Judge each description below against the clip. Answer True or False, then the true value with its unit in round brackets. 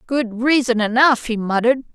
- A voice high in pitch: True (240 Hz)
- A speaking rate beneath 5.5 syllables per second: True (5.2 syllables/s)